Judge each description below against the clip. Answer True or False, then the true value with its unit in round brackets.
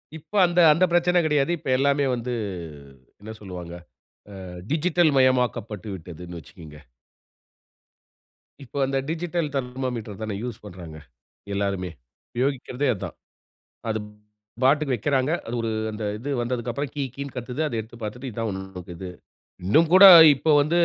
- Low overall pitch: True (125 Hz)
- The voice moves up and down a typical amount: False (5.9 semitones)